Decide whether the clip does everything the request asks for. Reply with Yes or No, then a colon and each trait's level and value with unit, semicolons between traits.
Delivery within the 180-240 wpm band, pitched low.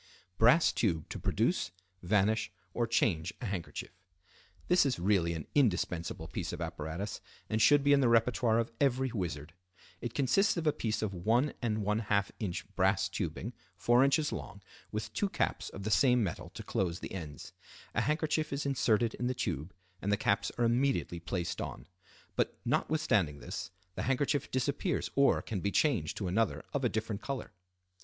No: average, 165 wpm; low, 110 Hz